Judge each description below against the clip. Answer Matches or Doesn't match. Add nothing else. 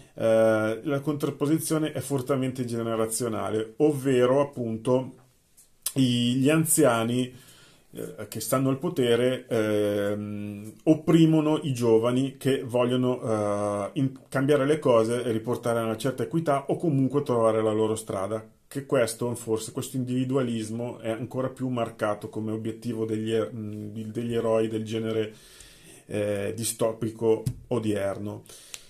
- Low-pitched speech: Matches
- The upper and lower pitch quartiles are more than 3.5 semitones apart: Doesn't match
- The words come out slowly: Matches